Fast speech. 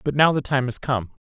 Yes: fast, 285 wpm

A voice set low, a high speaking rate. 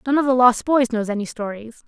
No: high, 240 Hz; fast, 255 wpm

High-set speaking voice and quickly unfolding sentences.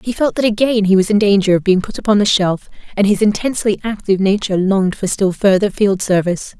Yes: high, 200 Hz; fast, 225 wpm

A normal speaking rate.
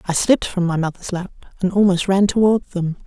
No: fast, 215 wpm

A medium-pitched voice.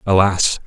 No: very low, 95 Hz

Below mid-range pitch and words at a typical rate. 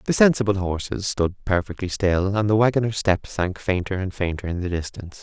Yes: very low, 95 Hz; average, 185 wpm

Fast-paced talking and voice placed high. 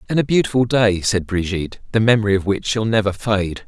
No: fast, 210 wpm; low, 105 Hz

